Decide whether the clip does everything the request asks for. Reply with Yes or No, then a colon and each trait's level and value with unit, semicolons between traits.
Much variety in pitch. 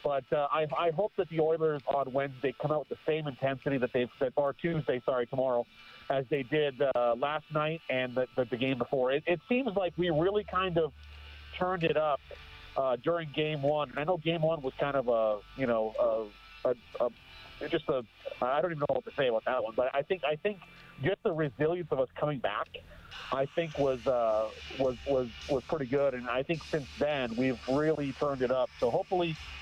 No: average, 4.0 semitones